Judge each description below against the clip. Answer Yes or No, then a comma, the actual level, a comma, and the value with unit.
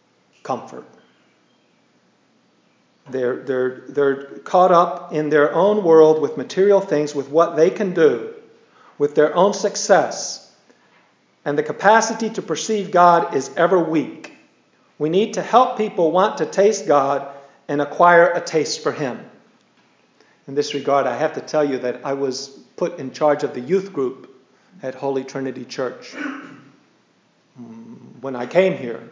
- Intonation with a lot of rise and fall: Yes, wide, 5.9 semitones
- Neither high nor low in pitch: Yes, medium, 160 Hz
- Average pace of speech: Yes, average, 150 wpm